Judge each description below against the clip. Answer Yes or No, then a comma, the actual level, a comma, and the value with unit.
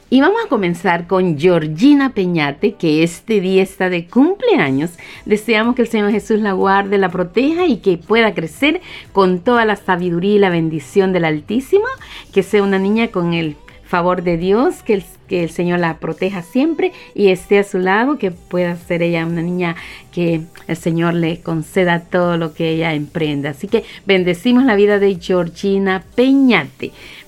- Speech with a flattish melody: No, average, 3.8 semitones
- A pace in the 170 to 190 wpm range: Yes, average, 180 wpm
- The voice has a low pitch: No, high, 190 Hz